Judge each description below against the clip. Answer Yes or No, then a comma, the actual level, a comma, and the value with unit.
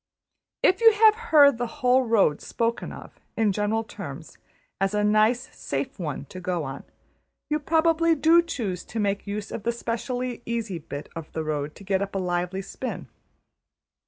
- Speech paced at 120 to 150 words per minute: No, average, 175 wpm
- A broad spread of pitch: Yes, wide, 5.8 semitones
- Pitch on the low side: No, high, 215 Hz